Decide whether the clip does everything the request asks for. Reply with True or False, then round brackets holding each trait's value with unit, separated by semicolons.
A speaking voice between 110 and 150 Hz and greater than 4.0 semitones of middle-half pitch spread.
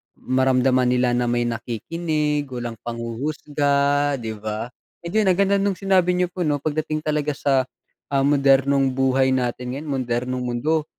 False (135 Hz; 3.5 semitones)